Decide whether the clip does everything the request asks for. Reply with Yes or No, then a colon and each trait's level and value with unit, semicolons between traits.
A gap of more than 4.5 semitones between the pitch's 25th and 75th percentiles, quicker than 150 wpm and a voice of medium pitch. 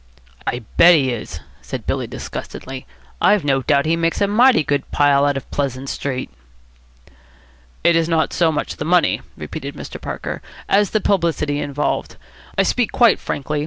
No: average, 3.9 semitones; average, 165 wpm; medium, 150 Hz